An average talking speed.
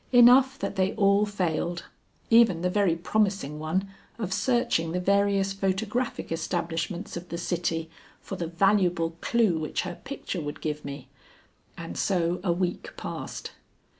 Yes: average, 145 wpm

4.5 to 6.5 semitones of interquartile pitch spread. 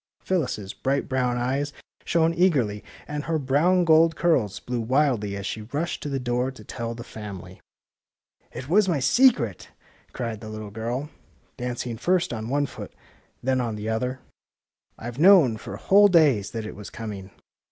Yes: wide, 5.5 semitones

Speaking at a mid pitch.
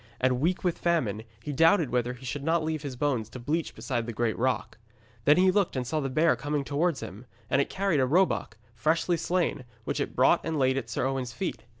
Yes: medium, 145 Hz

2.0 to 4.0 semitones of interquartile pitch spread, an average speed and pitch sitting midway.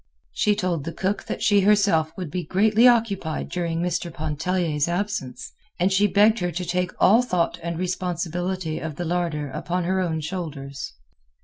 Yes: average, 2.9 semitones; average, 170 wpm; medium, 180 Hz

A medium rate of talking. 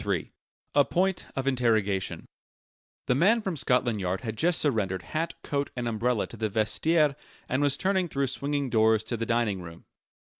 Yes: average, 175 wpm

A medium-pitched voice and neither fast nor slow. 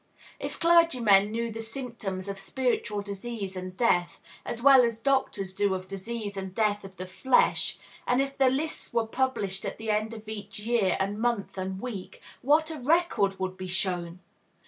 No: high, 215 Hz; average, 175 wpm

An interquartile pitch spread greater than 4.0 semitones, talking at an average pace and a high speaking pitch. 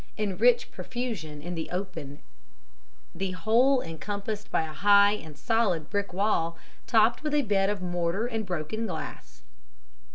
Yes: average, 4.6 semitones; average, 150 wpm; high, 200 Hz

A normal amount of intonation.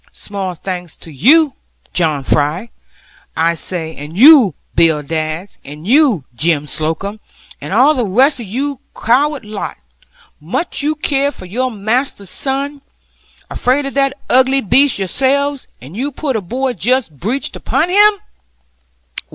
No: wide, 8.3 semitones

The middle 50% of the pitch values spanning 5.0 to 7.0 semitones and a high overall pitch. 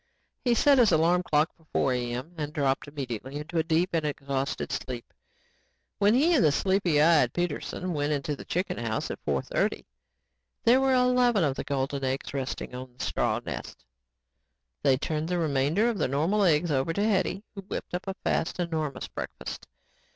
No: wide, 5.4 semitones; medium, 155 Hz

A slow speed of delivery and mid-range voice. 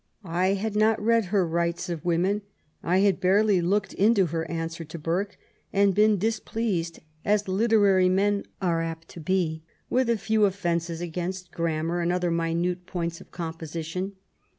No: average, 160 wpm; medium, 180 Hz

